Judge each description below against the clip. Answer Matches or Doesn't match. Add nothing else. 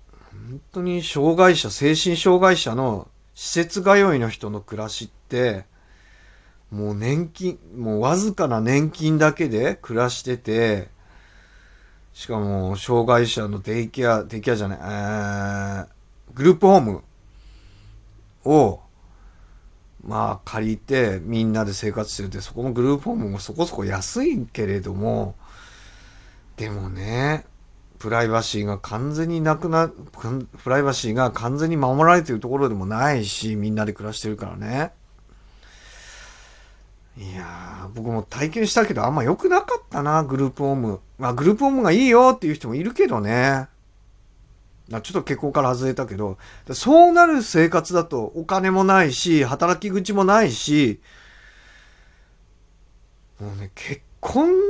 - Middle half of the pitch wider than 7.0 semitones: Matches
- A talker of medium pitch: Doesn't match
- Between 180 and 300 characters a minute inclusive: Matches